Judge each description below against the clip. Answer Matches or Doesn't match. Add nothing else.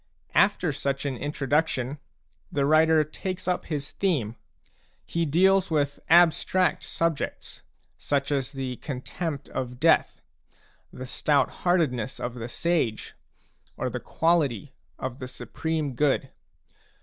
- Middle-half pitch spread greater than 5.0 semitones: Doesn't match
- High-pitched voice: Doesn't match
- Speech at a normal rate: Doesn't match